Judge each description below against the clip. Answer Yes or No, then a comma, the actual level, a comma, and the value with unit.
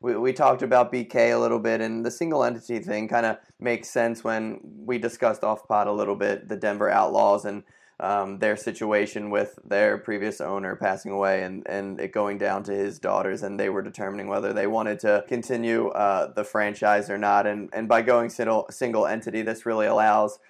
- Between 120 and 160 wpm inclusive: No, average, 200 wpm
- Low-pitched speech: Yes, low, 110 Hz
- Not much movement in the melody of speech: Yes, narrow, 2.2 semitones